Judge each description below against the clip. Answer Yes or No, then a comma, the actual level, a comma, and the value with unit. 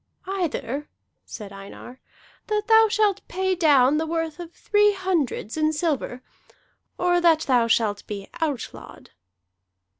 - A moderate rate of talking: No, slow, 125 wpm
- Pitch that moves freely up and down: Yes, wide, 6.9 semitones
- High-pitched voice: Yes, very high, 320 Hz